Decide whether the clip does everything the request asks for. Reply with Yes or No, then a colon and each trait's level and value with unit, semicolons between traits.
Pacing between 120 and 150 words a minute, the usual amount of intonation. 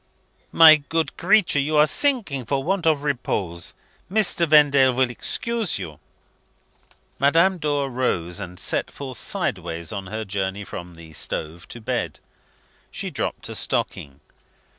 No: average, 140 wpm; wide, 8.6 semitones